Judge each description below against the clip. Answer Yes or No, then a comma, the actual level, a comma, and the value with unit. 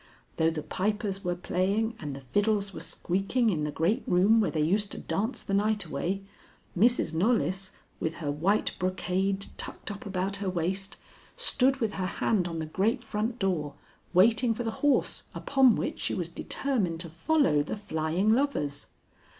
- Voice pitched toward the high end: Yes, high, 195 Hz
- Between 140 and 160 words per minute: No, average, 175 wpm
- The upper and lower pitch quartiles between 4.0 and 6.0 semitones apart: Yes, average, 4.3 semitones